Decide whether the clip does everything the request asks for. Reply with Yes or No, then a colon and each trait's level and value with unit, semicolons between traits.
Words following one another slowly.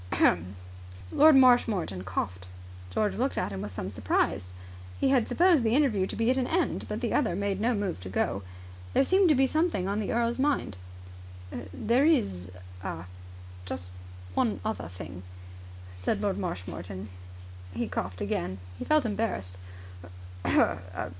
No: average, 150 wpm